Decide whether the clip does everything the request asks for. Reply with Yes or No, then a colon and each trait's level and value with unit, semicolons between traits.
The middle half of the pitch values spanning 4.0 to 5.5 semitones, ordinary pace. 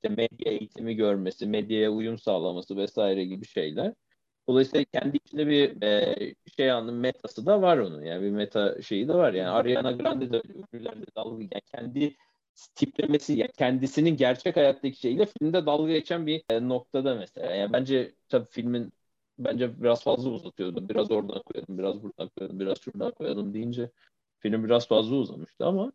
No: average, 5.2 semitones; fast, 155 wpm